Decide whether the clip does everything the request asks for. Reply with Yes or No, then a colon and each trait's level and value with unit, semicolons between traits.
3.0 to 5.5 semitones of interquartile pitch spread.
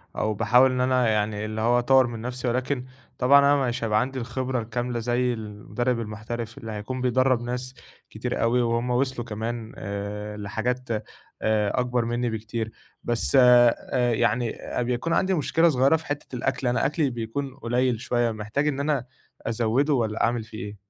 No: narrow, 2.5 semitones